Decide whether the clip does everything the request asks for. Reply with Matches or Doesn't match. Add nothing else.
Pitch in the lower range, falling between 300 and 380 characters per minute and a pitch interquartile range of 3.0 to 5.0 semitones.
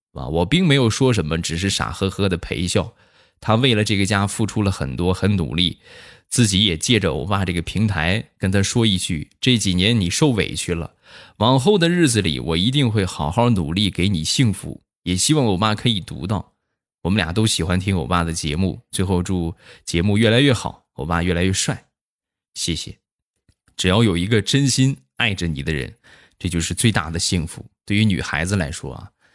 Doesn't match